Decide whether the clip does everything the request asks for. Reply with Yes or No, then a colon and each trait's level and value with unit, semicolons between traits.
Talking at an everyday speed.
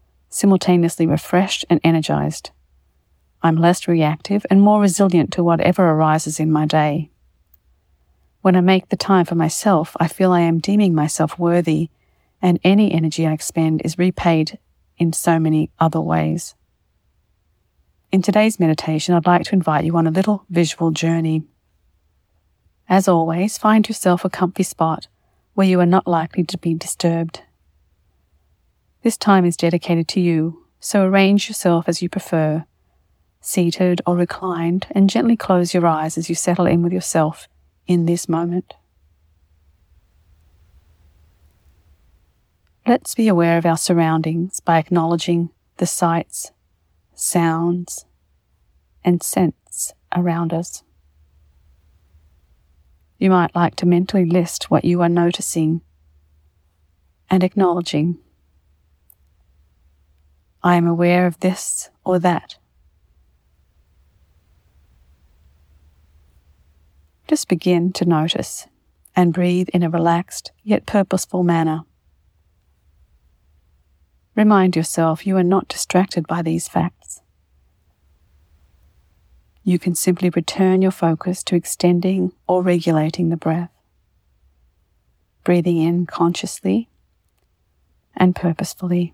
No: slow, 115 wpm